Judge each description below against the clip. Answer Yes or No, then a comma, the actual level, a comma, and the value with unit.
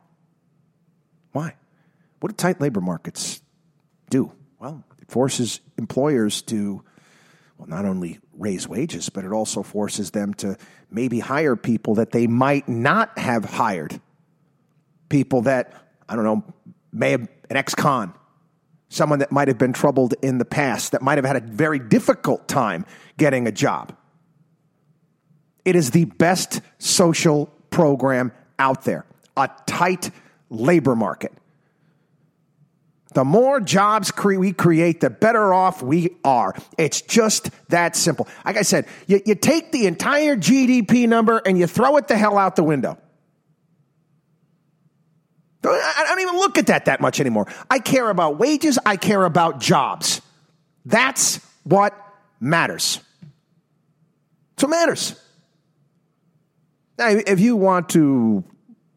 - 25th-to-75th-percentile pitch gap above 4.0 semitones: Yes, average, 4.6 semitones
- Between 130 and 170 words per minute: Yes, average, 140 wpm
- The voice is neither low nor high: Yes, medium, 160 Hz